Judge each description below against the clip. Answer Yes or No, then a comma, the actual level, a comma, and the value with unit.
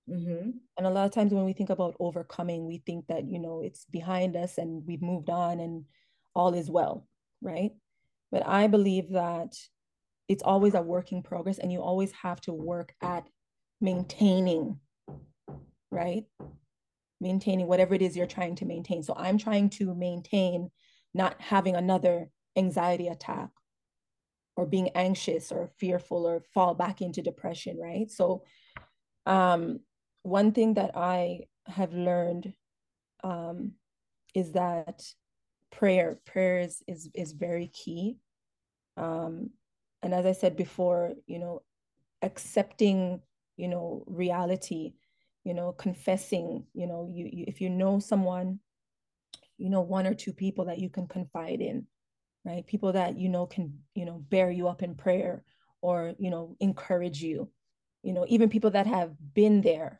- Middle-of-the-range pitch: Yes, medium, 180 Hz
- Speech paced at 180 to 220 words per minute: No, average, 150 wpm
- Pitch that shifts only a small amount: Yes, narrow, 1.8 semitones